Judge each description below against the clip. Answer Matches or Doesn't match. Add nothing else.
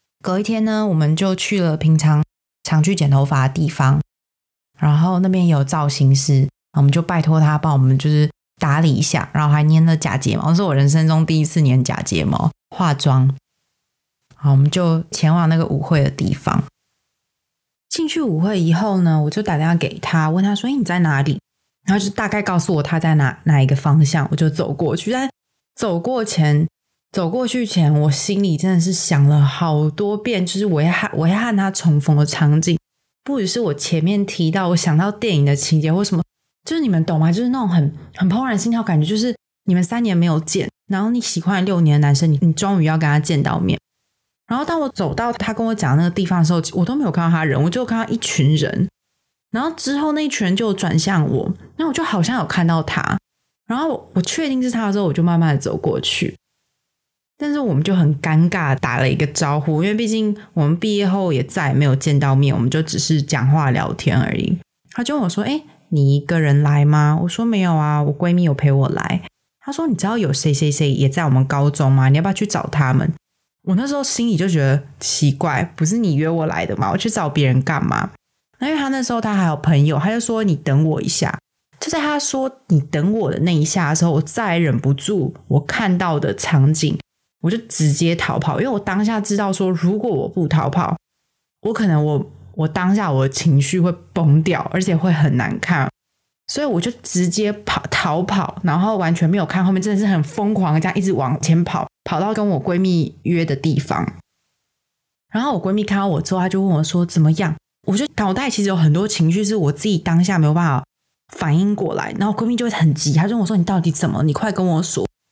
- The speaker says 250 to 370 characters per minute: Matches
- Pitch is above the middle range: Doesn't match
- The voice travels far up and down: Doesn't match